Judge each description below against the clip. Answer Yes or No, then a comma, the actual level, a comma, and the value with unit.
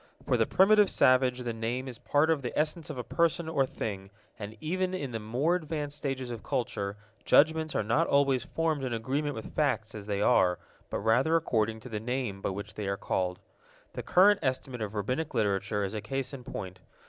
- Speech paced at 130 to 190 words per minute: No, fast, 205 wpm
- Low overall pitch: Yes, low, 125 Hz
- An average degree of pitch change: No, wide, 5.8 semitones